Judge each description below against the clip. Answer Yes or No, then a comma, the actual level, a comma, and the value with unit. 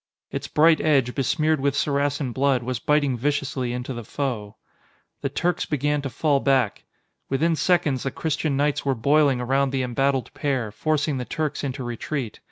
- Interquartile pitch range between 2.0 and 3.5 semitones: Yes, narrow, 2.5 semitones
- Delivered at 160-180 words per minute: Yes, average, 170 wpm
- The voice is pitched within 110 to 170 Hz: Yes, medium, 140 Hz